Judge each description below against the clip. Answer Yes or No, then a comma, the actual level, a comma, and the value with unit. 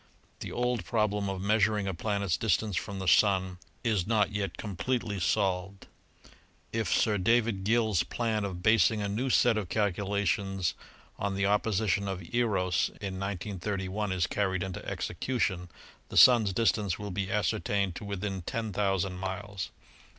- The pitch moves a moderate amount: No, narrow, 2.2 semitones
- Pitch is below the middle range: Yes, low, 100 Hz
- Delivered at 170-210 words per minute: No, average, 150 wpm